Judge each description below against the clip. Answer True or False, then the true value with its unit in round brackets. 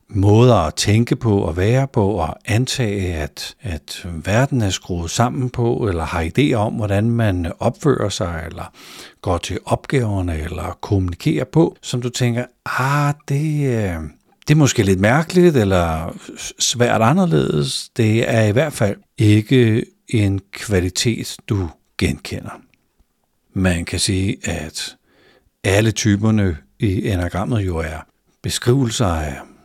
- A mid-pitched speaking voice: False (105 Hz)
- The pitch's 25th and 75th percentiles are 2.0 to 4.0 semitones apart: False (5.2 semitones)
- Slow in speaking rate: True (135 wpm)